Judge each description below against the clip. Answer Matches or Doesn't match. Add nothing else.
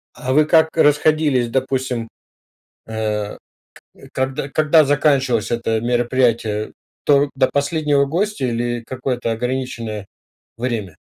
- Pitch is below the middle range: Matches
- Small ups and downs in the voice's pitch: Doesn't match